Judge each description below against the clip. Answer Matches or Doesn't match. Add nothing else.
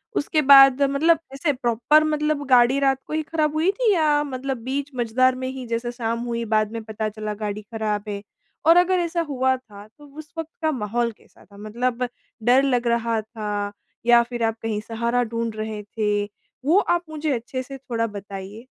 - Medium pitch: Doesn't match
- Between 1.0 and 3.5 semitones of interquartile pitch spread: Doesn't match